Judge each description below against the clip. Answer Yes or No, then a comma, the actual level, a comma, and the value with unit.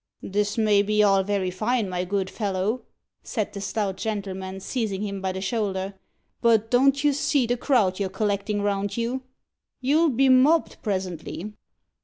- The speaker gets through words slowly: No, average, 160 wpm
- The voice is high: Yes, high, 205 Hz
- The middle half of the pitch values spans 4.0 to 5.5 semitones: No, average, 3.5 semitones